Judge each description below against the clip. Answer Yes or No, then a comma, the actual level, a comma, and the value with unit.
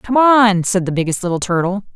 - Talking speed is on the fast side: Yes, fast, 215 wpm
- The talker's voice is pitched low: No, high, 200 Hz